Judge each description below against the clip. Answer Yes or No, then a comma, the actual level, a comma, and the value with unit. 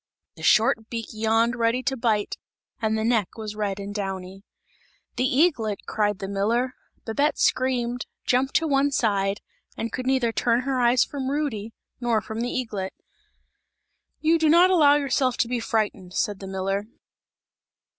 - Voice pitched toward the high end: Yes, high, 230 Hz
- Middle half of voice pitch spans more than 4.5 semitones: No, average, 3.7 semitones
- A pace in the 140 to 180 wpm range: Yes, average, 160 wpm